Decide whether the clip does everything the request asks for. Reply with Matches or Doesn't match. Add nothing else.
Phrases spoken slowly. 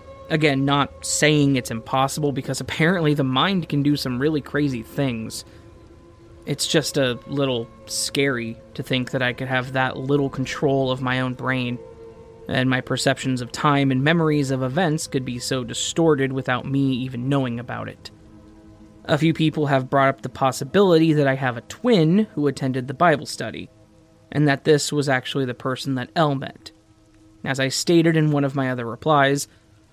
Doesn't match